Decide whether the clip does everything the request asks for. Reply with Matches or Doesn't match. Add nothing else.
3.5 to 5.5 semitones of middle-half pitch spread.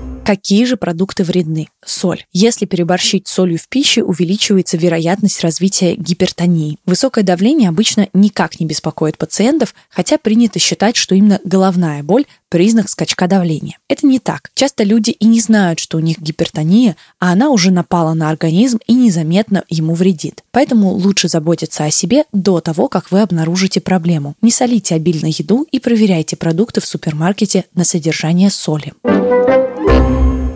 Matches